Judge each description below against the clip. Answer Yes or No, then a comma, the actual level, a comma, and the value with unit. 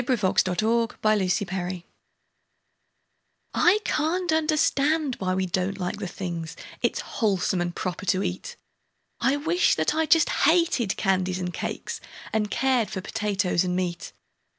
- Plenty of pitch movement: Yes, wide, 7.4 semitones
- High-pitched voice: Yes, high, 205 Hz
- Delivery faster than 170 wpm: No, average, 145 wpm